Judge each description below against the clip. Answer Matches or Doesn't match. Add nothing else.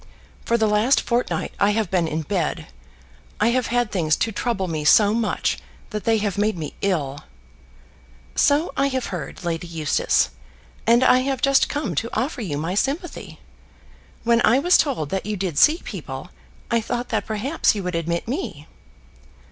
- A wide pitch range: Matches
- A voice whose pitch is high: Matches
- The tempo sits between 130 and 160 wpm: Doesn't match